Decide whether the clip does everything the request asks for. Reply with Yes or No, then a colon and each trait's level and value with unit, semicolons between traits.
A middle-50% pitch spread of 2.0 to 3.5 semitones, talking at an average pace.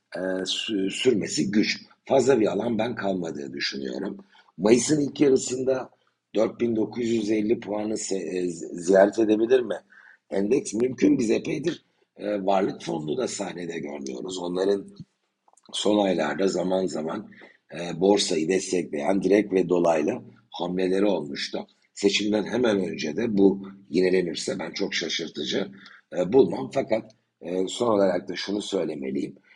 Yes: narrow, 2.6 semitones; average, 110 wpm